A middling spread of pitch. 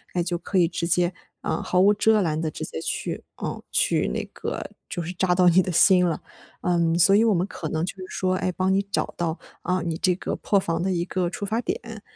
No: narrow, 2.0 semitones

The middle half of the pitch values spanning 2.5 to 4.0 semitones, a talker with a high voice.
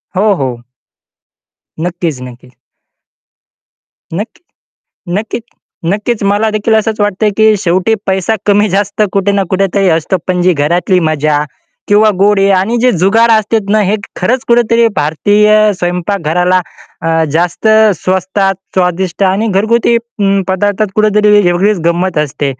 Yes: average, 3.1 semitones; high, 195 Hz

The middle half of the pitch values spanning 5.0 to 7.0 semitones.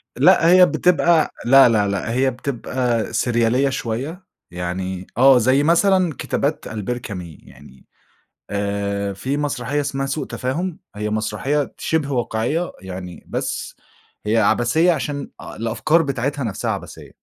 Yes: wide, 5.5 semitones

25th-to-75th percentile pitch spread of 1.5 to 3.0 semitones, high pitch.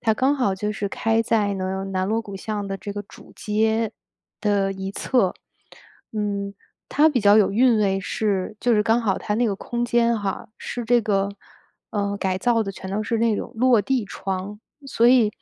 Yes: narrow, 2.6 semitones; high, 210 Hz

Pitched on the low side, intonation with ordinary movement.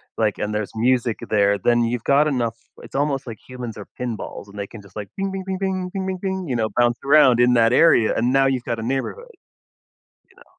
Yes: low, 120 Hz; average, 4.0 semitones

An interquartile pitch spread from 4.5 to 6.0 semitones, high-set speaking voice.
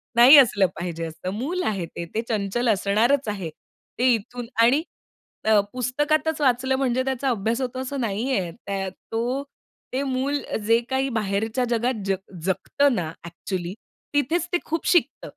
Yes: average, 5.1 semitones; high, 240 Hz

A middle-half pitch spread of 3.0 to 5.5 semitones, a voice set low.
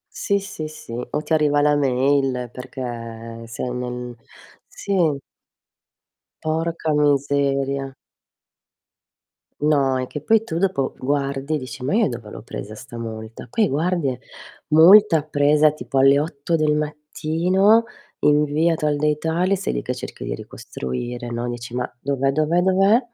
No: average, 4.0 semitones; medium, 145 Hz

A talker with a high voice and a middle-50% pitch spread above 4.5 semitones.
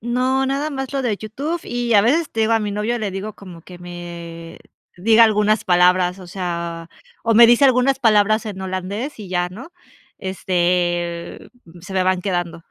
Yes: high, 200 Hz; average, 4.9 semitones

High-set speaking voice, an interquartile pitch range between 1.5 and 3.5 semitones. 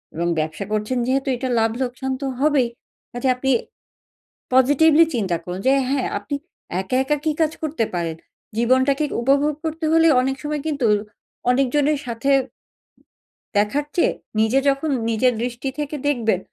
No: very high, 260 Hz; average, 4.0 semitones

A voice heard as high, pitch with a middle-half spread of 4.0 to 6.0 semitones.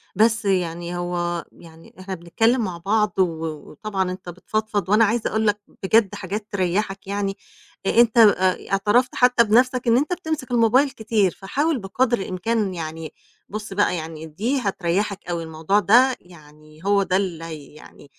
Yes: high, 195 Hz; average, 4.4 semitones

